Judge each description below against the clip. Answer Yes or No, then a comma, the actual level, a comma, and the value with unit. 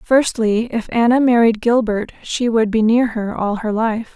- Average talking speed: Yes, average, 190 wpm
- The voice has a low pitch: No, high, 225 Hz